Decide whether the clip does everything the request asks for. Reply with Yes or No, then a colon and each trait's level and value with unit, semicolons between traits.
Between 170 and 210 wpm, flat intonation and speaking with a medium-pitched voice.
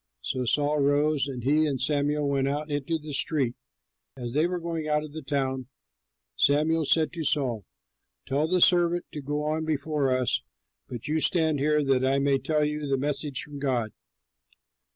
Yes: average, 180 wpm; narrow, 2.2 semitones; medium, 145 Hz